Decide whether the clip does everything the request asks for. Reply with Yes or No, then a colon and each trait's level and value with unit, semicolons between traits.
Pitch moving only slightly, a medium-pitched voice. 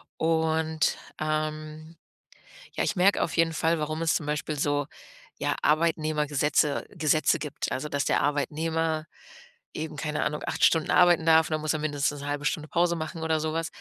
Yes: narrow, 1.3 semitones; medium, 155 Hz